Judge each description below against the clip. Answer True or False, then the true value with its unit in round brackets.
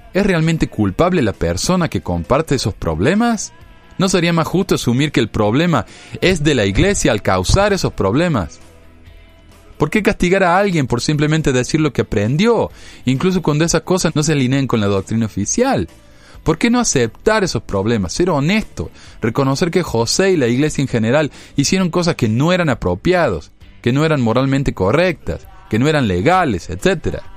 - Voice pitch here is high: False (135 Hz)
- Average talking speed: True (175 wpm)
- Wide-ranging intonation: True (8.5 semitones)